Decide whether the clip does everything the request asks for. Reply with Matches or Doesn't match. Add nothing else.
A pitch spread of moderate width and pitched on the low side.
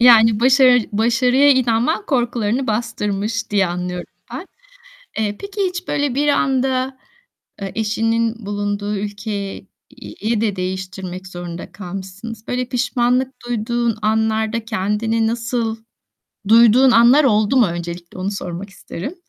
Doesn't match